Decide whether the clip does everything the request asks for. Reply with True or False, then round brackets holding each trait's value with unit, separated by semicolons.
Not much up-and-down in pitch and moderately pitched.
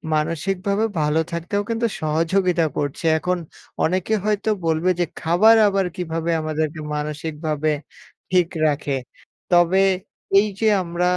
False (3.5 semitones; 170 Hz)